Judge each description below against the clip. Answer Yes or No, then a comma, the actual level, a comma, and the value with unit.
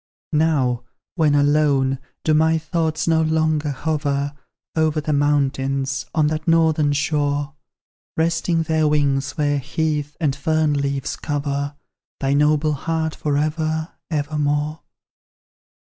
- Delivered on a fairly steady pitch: Yes, narrow, 1.7 semitones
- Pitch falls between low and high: Yes, medium, 150 Hz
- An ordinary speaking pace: No, slow, 120 wpm